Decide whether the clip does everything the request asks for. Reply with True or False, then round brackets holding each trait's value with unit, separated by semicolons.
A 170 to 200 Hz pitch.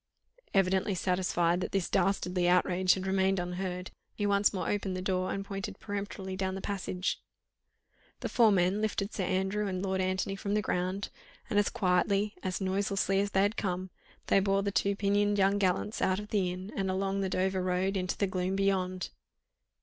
True (190 Hz)